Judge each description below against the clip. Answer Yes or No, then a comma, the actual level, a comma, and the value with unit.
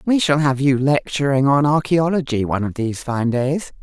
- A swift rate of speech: No, average, 190 wpm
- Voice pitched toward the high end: No, medium, 140 Hz